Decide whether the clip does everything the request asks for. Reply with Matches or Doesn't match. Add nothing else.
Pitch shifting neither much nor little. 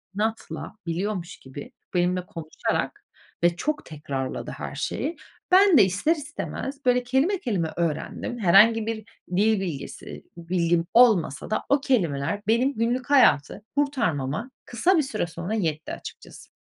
Doesn't match